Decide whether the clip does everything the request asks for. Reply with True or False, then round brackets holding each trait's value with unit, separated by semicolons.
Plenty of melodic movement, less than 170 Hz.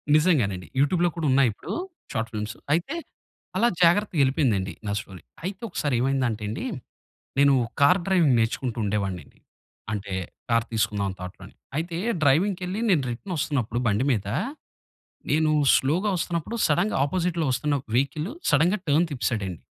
True (7.8 semitones; 140 Hz)